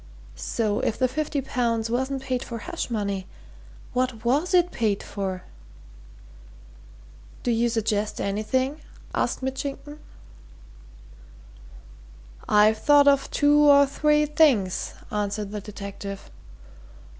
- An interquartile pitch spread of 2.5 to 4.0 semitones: No, average, 5.2 semitones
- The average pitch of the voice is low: No, high, 240 Hz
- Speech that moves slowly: Yes, slow, 110 wpm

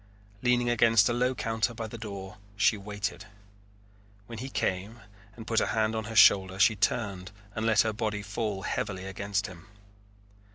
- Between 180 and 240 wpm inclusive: No, average, 170 wpm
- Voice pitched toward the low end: Yes, low, 105 Hz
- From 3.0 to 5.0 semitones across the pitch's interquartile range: No, narrow, 2.4 semitones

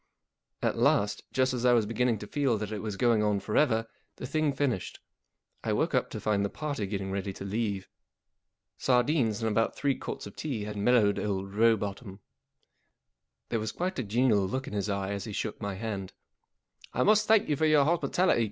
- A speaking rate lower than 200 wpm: No, fast, 205 wpm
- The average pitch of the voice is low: Yes, low, 110 Hz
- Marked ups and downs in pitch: No, average, 4.3 semitones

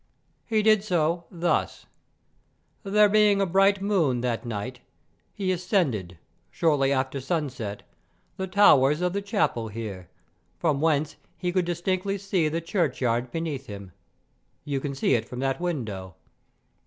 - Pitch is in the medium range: Yes, medium, 160 Hz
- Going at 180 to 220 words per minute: No, average, 140 wpm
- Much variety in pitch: Yes, wide, 6.9 semitones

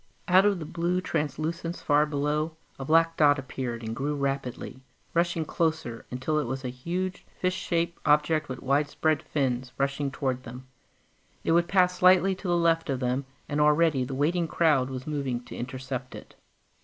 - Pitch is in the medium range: Yes, medium, 150 Hz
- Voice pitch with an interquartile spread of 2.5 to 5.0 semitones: Yes, average, 4.2 semitones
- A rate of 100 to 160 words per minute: No, average, 175 wpm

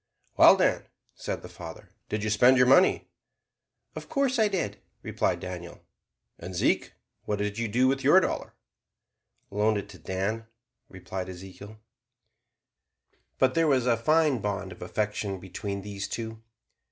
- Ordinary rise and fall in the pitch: Yes, average, 4.9 semitones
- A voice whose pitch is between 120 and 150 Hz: No, low, 105 Hz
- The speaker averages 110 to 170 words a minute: Yes, average, 150 wpm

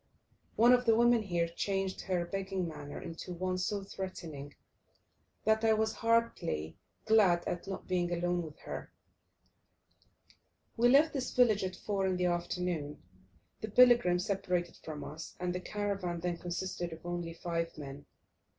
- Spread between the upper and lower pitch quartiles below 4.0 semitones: Yes, average, 3.3 semitones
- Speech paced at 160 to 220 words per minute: No, average, 150 wpm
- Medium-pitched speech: Yes, medium, 180 Hz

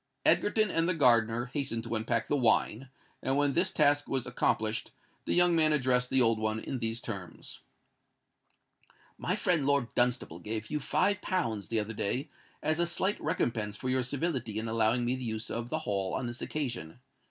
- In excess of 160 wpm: Yes, average, 185 wpm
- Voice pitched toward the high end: No, low, 125 Hz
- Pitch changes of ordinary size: Yes, average, 4.5 semitones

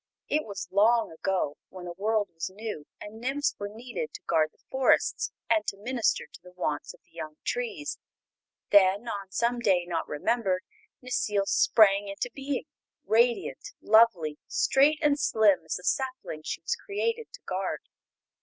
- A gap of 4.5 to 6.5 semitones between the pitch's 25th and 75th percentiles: Yes, average, 5.1 semitones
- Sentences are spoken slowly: No, average, 165 wpm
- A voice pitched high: Yes, high, 210 Hz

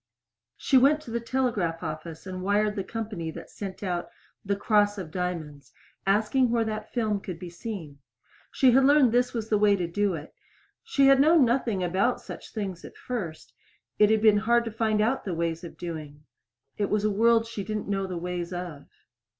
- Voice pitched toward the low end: No, high, 205 Hz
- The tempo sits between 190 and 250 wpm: Yes, average, 200 wpm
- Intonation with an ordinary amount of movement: Yes, average, 4.5 semitones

